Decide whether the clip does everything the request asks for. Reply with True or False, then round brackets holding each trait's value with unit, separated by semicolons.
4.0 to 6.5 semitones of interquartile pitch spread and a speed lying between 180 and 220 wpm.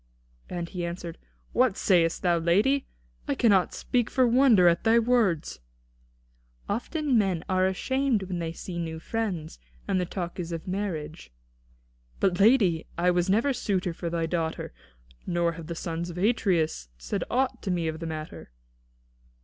False (4.7 semitones; 160 wpm)